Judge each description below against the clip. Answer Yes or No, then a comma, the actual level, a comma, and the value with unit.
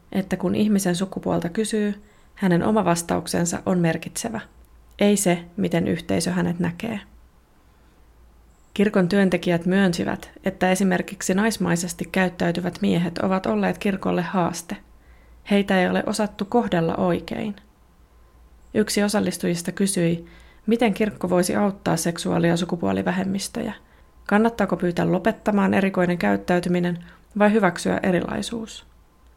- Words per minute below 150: Yes, average, 105 wpm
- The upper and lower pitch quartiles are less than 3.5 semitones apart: Yes, average, 3.0 semitones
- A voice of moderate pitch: Yes, medium, 180 Hz